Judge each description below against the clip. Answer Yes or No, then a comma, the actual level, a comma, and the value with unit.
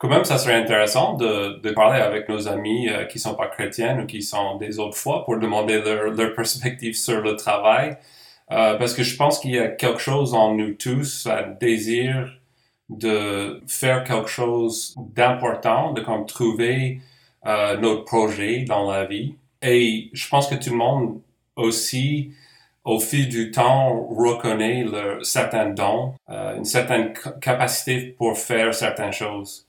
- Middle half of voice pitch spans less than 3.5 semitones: Yes, average, 2.9 semitones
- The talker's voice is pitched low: Yes, low, 115 Hz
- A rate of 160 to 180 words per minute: Yes, average, 170 wpm